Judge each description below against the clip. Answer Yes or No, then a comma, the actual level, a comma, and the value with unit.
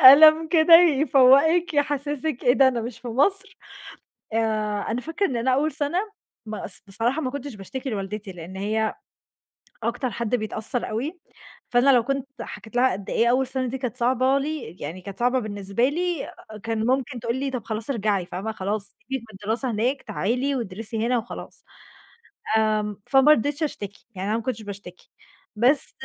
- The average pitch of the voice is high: Yes, high, 245 Hz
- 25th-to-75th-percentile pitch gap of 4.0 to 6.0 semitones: Yes, average, 4.3 semitones